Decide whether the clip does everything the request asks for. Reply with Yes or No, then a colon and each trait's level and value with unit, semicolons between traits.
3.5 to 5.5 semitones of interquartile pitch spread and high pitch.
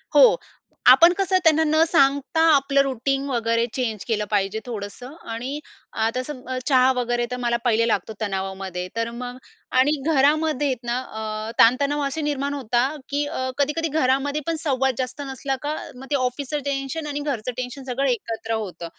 Yes: average, 3.8 semitones; very high, 260 Hz